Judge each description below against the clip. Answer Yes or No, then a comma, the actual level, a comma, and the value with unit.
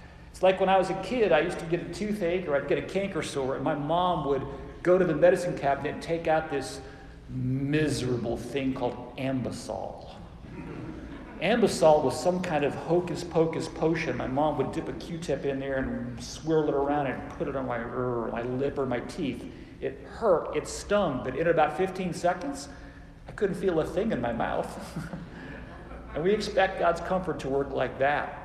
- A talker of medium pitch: Yes, medium, 155 Hz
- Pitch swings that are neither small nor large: Yes, average, 4.8 semitones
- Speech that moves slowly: No, average, 200 wpm